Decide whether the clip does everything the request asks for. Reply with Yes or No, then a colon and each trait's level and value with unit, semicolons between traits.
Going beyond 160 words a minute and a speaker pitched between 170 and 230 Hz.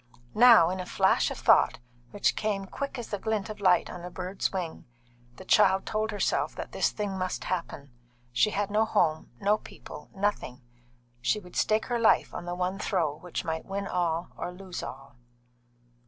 Yes: average, 185 wpm; high, 190 Hz